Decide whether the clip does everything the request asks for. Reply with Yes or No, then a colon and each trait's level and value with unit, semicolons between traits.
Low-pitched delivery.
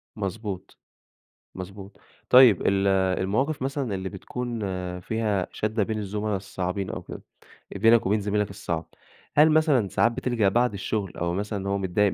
Yes: low, 105 Hz